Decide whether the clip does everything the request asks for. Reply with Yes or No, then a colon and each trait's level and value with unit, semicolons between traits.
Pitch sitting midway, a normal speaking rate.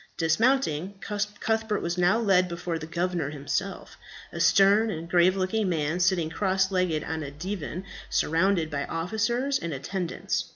Yes: medium, 180 Hz; average, 150 wpm